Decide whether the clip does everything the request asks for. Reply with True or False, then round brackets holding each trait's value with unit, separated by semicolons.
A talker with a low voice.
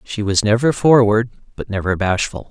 True (110 Hz)